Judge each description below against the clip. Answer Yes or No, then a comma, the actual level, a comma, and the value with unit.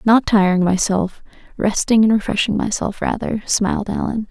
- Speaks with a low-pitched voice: No, high, 210 Hz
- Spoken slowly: Yes, slow, 125 wpm